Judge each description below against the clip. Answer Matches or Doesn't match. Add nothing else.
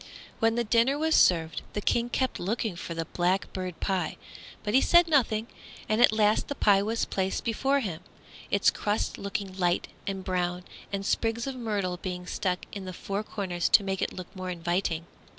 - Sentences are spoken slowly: Doesn't match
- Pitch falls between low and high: Doesn't match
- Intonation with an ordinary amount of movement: Matches